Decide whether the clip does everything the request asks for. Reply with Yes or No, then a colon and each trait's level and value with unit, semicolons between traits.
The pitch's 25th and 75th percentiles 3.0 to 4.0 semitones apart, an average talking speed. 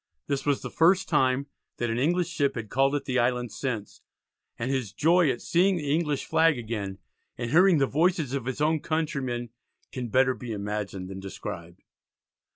No: average, 4.9 semitones; average, 180 wpm